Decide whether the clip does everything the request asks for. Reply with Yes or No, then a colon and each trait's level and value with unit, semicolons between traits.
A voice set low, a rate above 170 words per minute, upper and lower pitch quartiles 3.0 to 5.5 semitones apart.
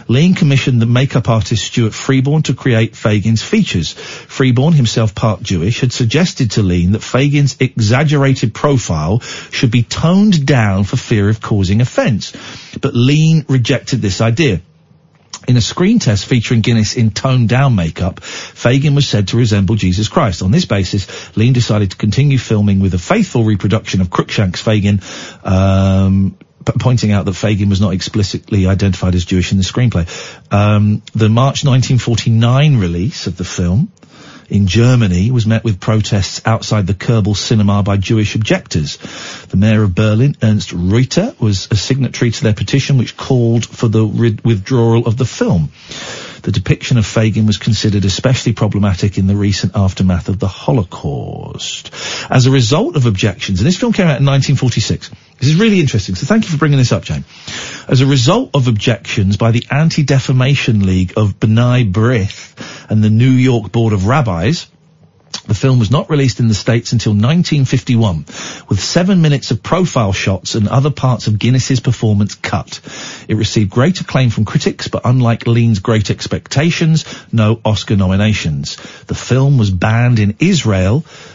No: low, 115 Hz; average, 165 wpm; average, 4.2 semitones